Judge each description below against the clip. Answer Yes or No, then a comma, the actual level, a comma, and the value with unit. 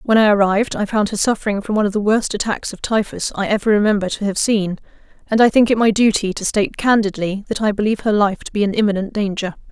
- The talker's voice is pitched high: Yes, high, 210 Hz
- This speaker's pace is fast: Yes, fast, 245 wpm